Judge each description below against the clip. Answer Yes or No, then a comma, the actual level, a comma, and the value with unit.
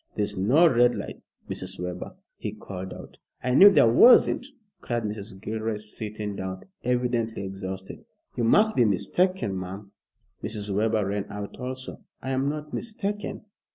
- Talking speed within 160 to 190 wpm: No, average, 150 wpm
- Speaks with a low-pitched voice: Yes, low, 110 Hz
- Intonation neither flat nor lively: Yes, average, 4.6 semitones